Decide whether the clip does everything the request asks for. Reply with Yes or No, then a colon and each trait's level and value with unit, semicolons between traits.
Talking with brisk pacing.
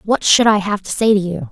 Yes: fast, 315 wpm